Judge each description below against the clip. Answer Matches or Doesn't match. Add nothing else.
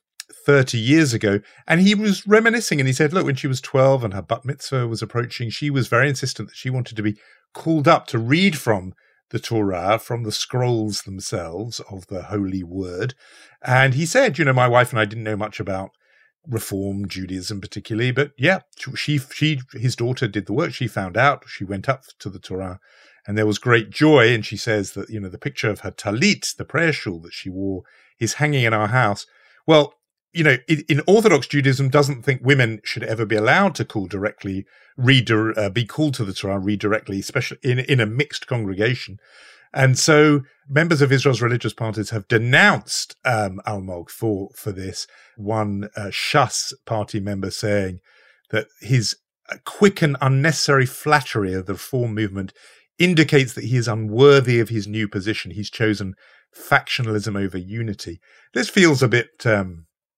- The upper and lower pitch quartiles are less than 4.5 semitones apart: Doesn't match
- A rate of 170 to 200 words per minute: Matches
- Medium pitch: Doesn't match